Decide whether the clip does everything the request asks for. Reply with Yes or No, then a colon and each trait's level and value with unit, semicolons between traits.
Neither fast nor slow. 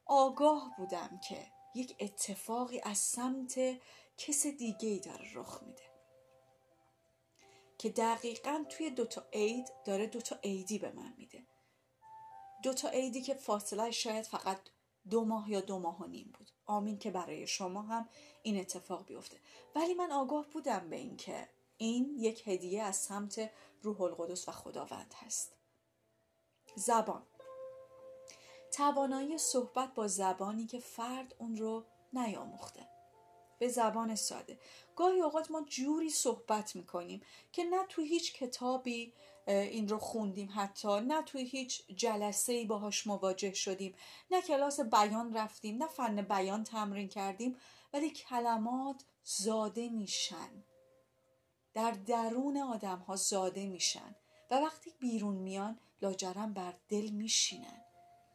Yes: average, 130 wpm